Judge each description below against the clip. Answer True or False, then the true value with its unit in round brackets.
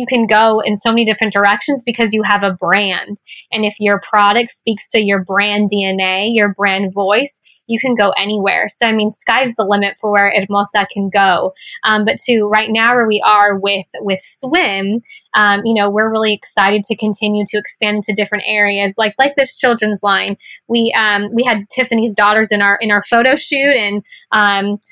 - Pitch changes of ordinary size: False (2.1 semitones)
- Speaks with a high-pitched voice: True (210 Hz)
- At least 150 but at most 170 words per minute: False (200 wpm)